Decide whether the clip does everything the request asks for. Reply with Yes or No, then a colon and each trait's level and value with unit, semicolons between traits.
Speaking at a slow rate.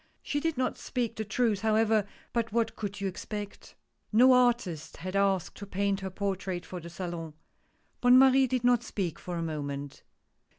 No: average, 180 wpm